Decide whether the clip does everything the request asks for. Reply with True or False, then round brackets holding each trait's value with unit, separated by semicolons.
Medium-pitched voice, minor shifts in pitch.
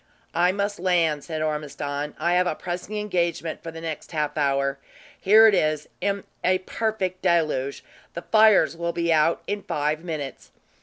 False (170 Hz; 3.5 semitones)